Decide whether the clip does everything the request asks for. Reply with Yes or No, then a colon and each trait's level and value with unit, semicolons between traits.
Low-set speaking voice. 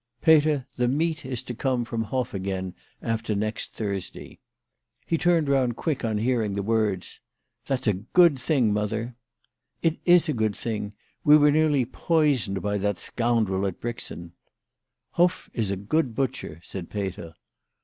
Yes: low, 115 Hz